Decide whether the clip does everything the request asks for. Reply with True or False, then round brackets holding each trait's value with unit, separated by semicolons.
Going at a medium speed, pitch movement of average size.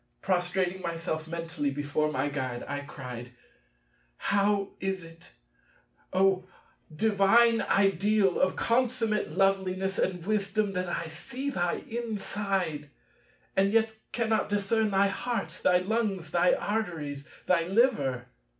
False (115 wpm; 4.1 semitones)